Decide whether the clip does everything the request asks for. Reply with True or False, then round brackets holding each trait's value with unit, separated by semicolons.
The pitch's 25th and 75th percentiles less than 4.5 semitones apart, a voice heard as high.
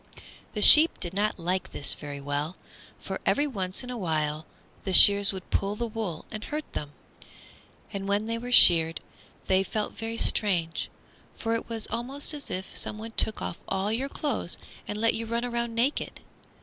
True (4.1 semitones; 210 Hz)